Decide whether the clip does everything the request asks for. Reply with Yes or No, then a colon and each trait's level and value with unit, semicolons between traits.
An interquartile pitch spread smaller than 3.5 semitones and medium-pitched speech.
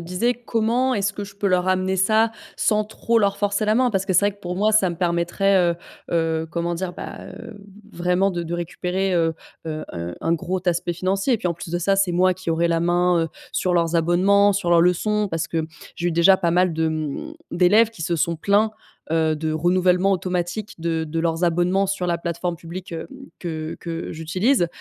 Yes: average, 2.8 semitones; medium, 180 Hz